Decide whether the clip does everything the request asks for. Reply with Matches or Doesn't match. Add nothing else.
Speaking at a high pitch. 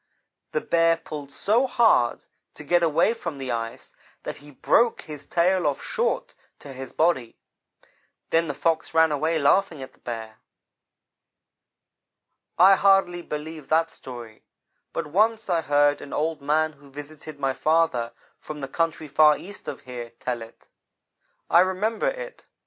Doesn't match